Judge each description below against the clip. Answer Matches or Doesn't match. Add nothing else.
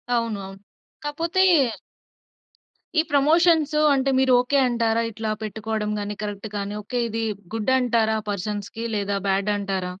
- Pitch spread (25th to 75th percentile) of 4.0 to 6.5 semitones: Matches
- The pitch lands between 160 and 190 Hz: Doesn't match